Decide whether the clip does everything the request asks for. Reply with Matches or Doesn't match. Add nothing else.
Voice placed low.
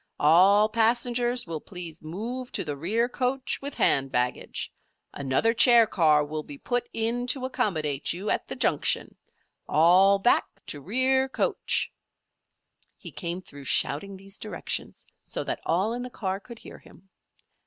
Doesn't match